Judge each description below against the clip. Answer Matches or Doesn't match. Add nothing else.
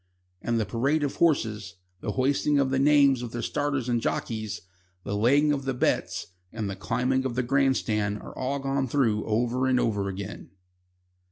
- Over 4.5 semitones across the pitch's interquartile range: Doesn't match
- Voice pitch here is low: Matches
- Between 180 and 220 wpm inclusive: Matches